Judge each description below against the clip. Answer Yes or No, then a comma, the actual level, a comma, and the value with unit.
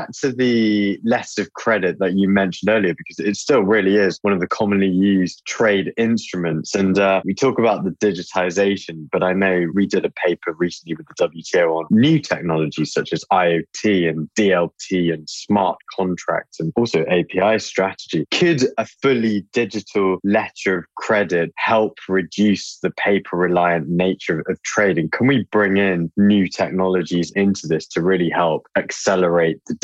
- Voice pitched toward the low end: Yes, very low, 95 Hz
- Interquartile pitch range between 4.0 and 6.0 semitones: No, average, 2.8 semitones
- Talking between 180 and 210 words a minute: No, average, 165 wpm